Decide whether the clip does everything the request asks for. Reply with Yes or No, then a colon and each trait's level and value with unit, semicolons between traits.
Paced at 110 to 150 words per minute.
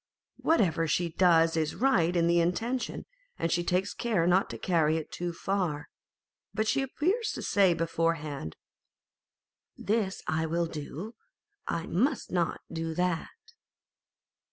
Yes: average, 140 wpm